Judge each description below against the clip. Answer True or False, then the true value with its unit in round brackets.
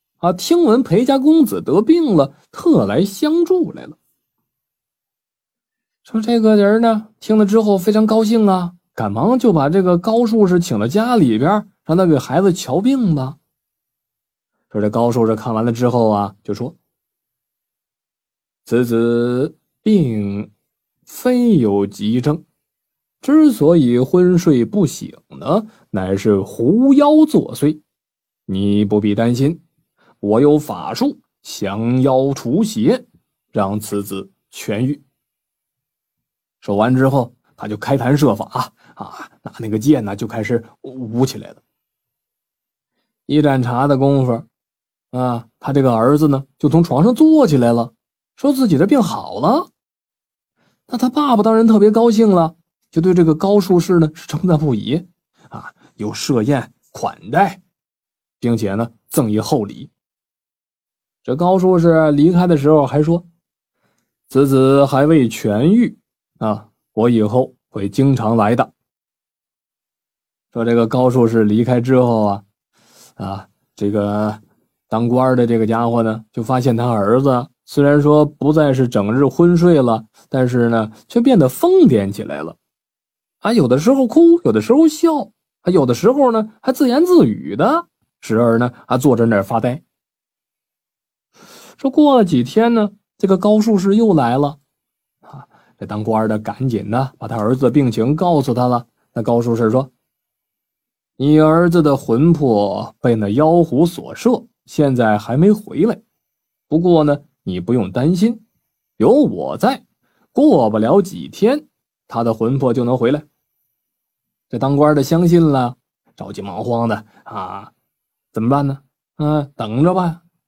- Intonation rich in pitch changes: True (7.7 semitones)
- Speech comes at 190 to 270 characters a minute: True (200 characters per minute)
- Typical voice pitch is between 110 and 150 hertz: True (140 Hz)